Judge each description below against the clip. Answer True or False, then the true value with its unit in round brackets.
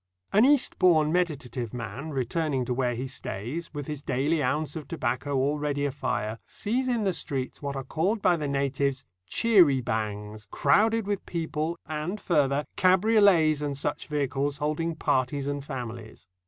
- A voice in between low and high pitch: True (145 Hz)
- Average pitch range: True (4.2 semitones)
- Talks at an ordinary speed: True (155 wpm)